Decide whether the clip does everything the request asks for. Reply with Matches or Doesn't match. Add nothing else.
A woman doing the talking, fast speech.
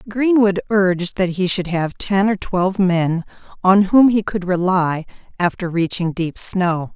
Doesn't match